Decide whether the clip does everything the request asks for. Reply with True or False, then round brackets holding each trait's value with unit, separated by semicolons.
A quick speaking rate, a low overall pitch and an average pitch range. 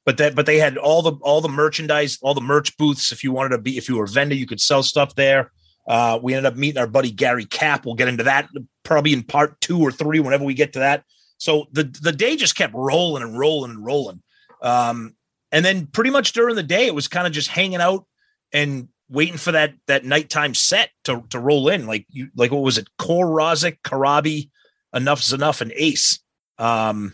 False (230 wpm; 145 Hz; 3.3 semitones)